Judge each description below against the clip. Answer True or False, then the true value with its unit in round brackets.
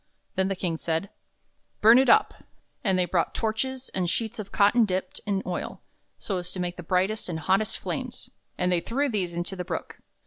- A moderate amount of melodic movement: True (3.4 semitones)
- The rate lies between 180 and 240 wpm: True (200 wpm)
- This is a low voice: False (190 Hz)